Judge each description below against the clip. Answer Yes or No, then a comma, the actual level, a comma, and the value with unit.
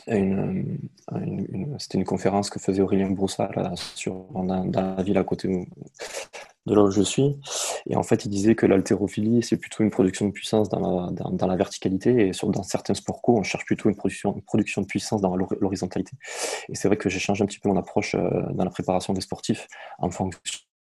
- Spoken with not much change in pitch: Yes, narrow, 1.9 semitones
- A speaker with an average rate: No, fast, 225 wpm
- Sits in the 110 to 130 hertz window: No, low, 100 Hz